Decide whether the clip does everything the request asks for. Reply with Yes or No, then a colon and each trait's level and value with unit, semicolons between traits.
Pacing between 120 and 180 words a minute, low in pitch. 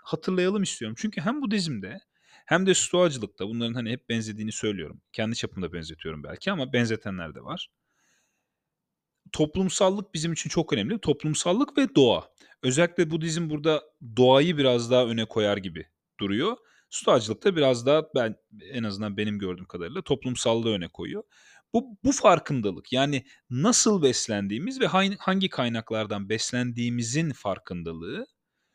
Yes: average, 135 wpm; low, 130 Hz